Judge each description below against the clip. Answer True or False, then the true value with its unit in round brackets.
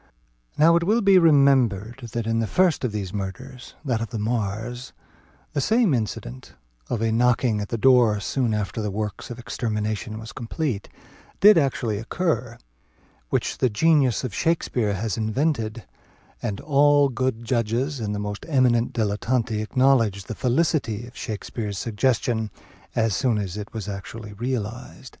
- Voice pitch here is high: False (115 Hz)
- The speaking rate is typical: True (155 wpm)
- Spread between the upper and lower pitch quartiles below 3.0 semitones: False (3.7 semitones)